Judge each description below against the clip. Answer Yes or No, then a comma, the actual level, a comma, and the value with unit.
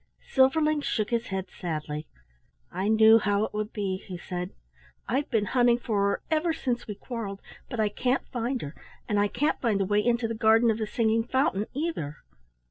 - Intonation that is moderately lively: Yes, average, 3.4 semitones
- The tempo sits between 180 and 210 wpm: Yes, average, 195 wpm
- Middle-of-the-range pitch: No, high, 220 Hz